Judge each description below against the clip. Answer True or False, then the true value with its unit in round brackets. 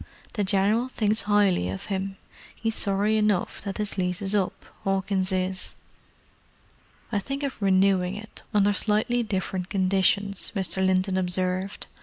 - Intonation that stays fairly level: True (1.9 semitones)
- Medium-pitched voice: False (195 Hz)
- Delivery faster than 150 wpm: False (140 wpm)